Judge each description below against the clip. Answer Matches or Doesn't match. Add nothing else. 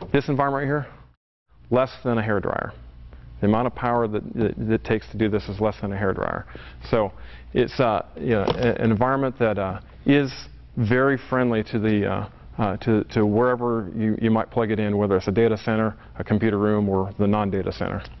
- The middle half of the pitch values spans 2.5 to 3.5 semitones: Matches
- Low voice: Matches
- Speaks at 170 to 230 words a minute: Matches